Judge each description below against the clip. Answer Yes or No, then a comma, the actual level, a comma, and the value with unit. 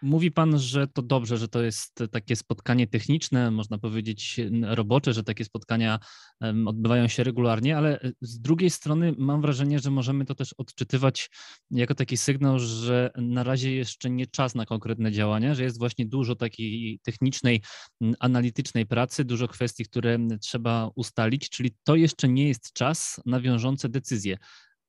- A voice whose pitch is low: Yes, low, 125 Hz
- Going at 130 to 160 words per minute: Yes, average, 155 wpm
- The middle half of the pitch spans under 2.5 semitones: No, average, 2.8 semitones